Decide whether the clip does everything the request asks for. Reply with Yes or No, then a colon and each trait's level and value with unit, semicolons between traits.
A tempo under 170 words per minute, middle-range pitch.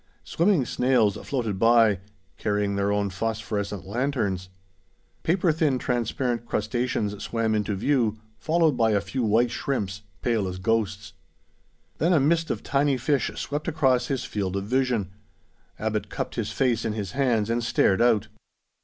No: average, 150 wpm; low, 115 Hz